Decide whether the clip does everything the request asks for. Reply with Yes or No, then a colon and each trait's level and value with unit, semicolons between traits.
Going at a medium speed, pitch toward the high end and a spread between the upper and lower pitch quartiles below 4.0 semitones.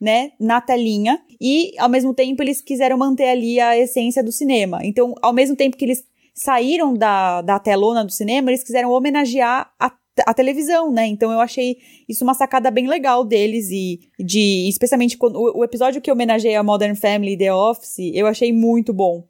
No: fast, 195 wpm; high, 245 Hz; average, 3.1 semitones